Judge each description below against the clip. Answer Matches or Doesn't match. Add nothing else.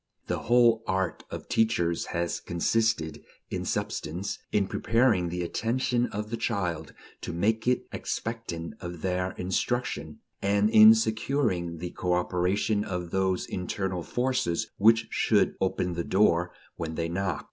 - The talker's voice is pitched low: Matches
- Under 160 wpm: Matches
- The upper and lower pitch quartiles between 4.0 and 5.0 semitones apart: Matches